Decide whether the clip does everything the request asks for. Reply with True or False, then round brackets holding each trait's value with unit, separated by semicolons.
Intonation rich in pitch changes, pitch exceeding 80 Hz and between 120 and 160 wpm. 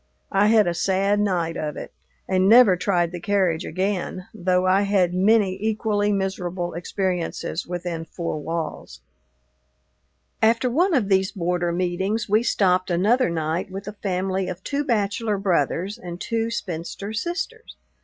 False (3.0 semitones; 190 Hz; 145 wpm)